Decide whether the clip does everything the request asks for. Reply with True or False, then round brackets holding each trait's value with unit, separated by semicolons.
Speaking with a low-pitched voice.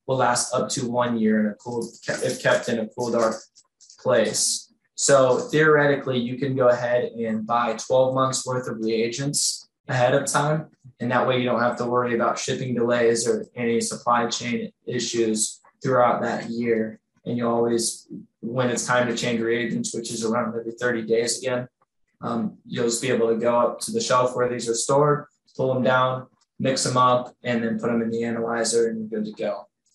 True (120 Hz)